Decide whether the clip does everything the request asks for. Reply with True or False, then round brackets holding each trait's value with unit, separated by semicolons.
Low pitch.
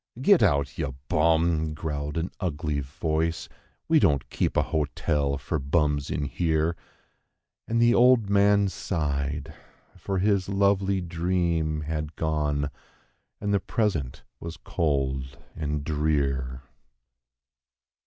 True (80 Hz)